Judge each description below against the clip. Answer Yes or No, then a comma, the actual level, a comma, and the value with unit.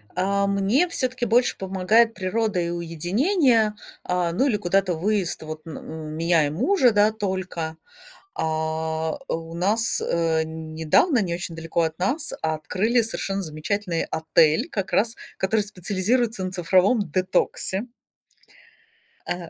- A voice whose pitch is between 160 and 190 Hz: Yes, medium, 185 Hz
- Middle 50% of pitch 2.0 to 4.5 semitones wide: No, average, 4.9 semitones